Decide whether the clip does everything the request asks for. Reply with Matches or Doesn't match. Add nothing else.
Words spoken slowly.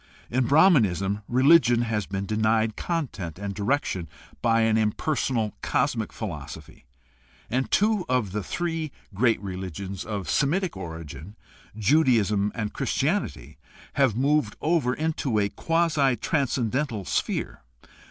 Matches